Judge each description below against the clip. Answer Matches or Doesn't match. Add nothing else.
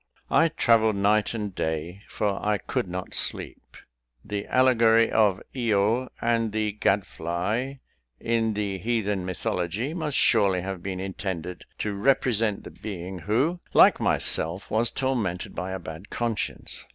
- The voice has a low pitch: Matches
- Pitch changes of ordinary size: Matches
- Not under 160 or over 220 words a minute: Doesn't match